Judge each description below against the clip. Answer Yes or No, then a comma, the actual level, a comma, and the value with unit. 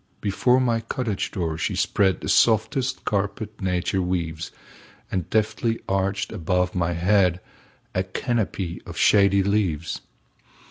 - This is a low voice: Yes, very low, 95 Hz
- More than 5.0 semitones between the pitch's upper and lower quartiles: No, average, 3.3 semitones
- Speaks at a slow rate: Yes, slow, 105 wpm